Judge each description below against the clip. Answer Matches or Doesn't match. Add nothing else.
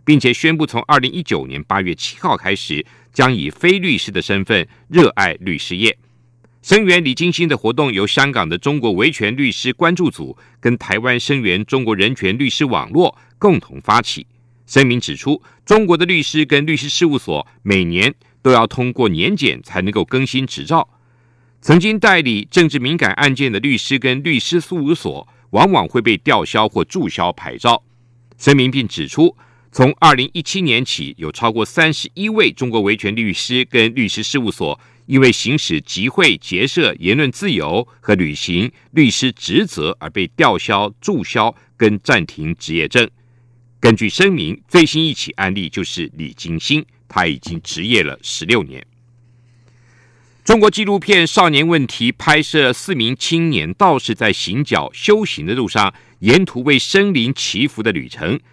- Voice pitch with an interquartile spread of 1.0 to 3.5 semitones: Doesn't match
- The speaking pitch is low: Matches